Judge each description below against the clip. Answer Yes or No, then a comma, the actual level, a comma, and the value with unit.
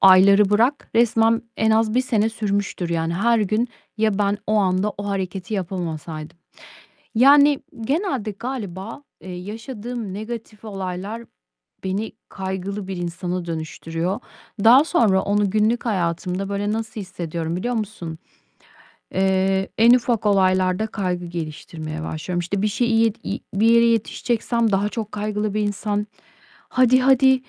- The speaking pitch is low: No, high, 205 Hz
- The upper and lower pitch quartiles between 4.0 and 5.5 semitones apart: No, average, 3.4 semitones